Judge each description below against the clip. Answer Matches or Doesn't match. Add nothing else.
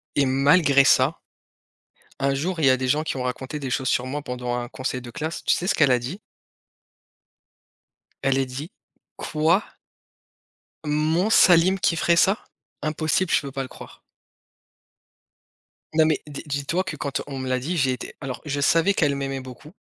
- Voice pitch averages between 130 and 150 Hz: Matches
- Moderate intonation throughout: Matches